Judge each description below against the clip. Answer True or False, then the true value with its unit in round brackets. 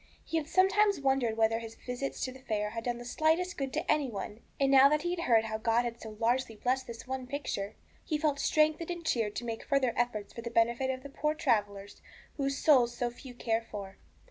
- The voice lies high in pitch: True (250 Hz)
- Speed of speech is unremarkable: False (225 wpm)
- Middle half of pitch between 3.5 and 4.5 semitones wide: True (4.1 semitones)